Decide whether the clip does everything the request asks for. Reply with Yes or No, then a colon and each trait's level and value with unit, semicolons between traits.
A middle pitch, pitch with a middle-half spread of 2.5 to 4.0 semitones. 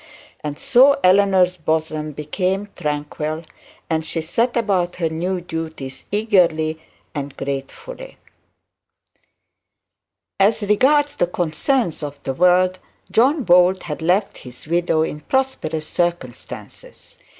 No: medium, 175 Hz; average, 4.6 semitones